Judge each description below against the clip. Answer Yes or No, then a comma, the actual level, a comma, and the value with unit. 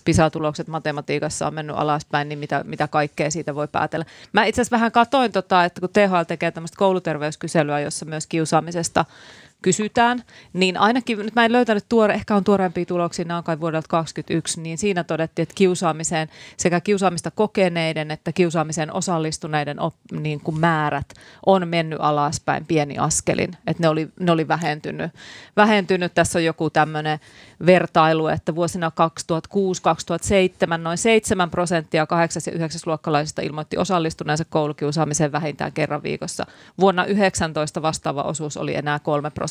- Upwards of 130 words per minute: Yes, average, 150 wpm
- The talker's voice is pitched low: No, medium, 165 Hz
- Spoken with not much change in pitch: No, average, 3.0 semitones